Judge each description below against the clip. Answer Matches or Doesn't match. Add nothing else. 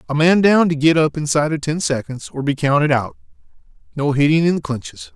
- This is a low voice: Doesn't match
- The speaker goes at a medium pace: Doesn't match